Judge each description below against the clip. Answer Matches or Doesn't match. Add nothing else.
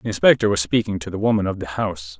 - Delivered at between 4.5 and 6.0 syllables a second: Doesn't match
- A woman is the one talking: Doesn't match